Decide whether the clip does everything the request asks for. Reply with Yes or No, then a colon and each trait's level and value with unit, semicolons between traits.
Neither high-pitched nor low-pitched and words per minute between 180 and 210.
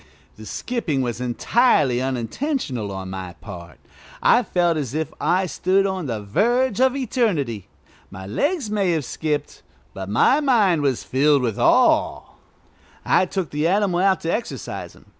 No: medium, 160 Hz; average, 155 wpm